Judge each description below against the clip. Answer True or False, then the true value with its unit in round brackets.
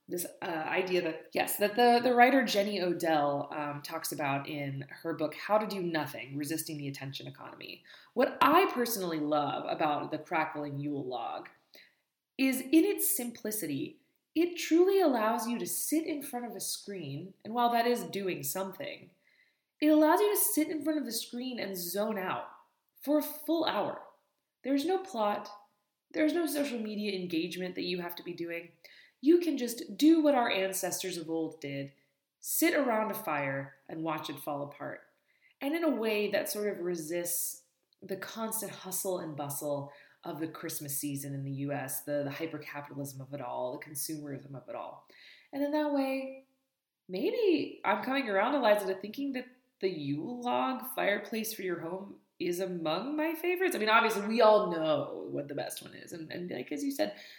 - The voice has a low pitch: False (200 Hz)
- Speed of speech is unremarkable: True (185 wpm)